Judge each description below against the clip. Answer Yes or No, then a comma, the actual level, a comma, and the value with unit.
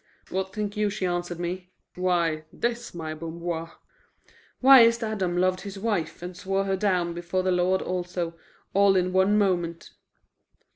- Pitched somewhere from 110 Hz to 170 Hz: No, medium, 185 Hz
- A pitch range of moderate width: No, narrow, 2.3 semitones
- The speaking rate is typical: Yes, average, 155 wpm